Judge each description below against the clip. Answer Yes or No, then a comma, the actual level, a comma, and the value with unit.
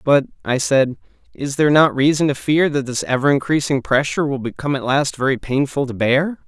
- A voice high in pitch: No, medium, 140 Hz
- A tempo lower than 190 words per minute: No, fast, 205 wpm